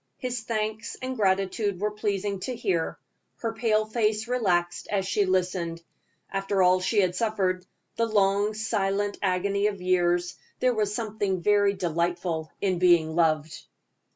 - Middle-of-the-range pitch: No, high, 195 Hz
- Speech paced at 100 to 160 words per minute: Yes, average, 145 wpm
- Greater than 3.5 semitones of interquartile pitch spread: No, average, 2.9 semitones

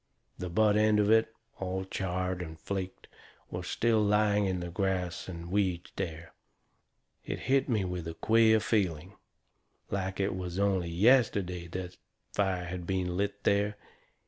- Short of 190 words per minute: Yes, average, 150 wpm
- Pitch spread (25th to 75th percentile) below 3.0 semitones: Yes, narrow, 2.5 semitones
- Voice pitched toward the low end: Yes, very low, 95 Hz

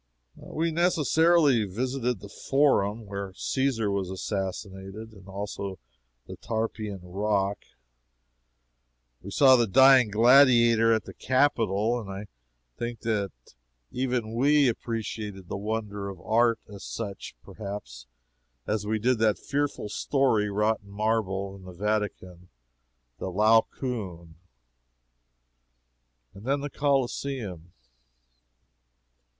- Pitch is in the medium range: No, low, 110 Hz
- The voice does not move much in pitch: No, average, 4.0 semitones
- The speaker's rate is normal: No, slow, 110 wpm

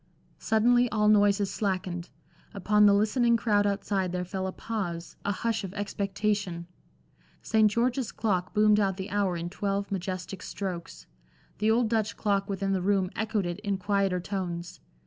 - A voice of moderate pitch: No, high, 200 Hz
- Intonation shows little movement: Yes, narrow, 2.2 semitones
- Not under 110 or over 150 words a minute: No, average, 160 wpm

